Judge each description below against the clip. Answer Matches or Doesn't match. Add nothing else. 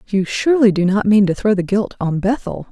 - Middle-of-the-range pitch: Doesn't match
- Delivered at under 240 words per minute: Doesn't match